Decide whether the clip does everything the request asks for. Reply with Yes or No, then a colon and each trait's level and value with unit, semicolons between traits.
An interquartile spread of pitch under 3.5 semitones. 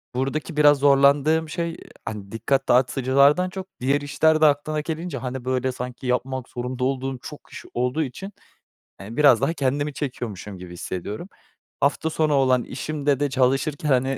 Yes: average, 2.9 semitones